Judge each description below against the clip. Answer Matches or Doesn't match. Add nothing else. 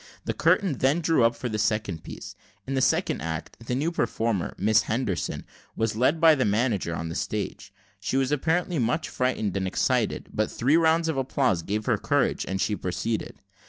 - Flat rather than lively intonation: Doesn't match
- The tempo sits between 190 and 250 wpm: Matches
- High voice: Doesn't match